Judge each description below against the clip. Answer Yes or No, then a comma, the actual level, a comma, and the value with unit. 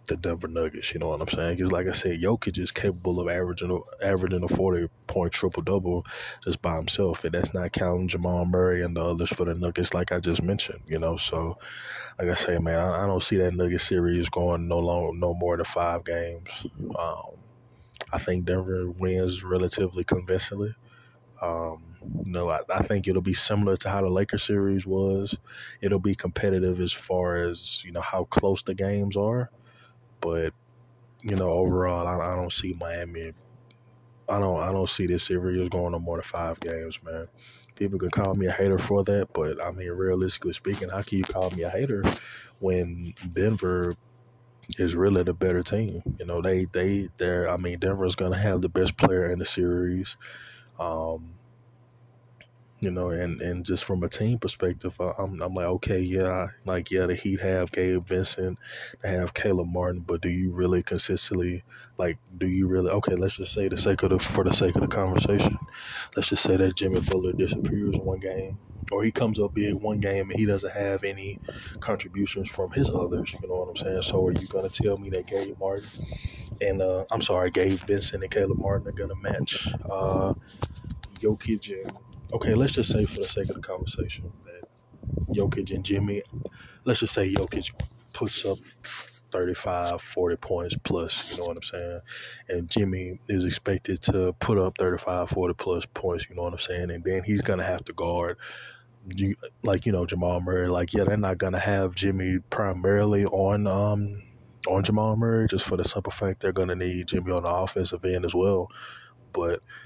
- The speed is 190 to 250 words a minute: Yes, average, 195 wpm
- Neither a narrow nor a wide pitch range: No, narrow, 2.1 semitones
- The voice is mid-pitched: No, very low, 95 Hz